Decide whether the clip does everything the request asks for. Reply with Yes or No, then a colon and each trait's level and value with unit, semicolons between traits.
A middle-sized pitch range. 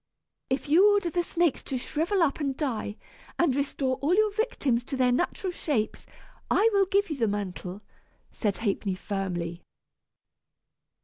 No: wide, 8.6 semitones